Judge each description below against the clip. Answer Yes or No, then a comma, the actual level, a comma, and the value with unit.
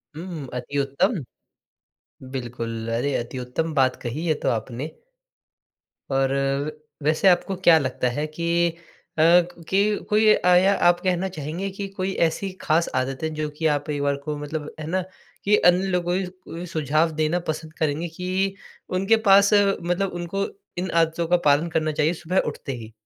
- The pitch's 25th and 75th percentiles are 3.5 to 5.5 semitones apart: Yes, average, 4.2 semitones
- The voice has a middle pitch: Yes, medium, 160 Hz